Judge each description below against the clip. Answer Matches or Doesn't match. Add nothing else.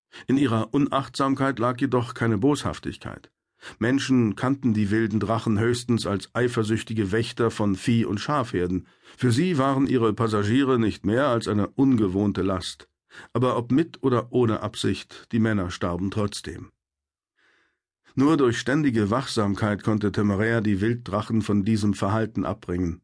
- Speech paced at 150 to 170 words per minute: Doesn't match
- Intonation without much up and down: Doesn't match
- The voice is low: Matches